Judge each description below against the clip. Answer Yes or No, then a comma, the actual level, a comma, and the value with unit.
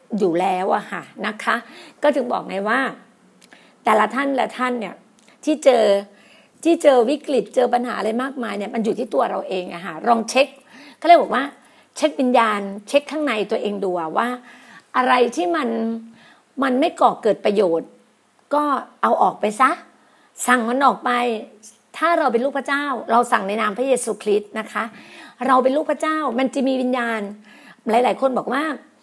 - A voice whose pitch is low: No, very high, 250 Hz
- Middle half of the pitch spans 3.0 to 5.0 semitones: Yes, average, 3.9 semitones